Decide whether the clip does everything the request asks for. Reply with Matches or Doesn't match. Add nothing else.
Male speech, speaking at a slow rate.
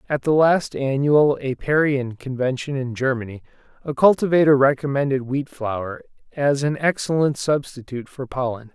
Matches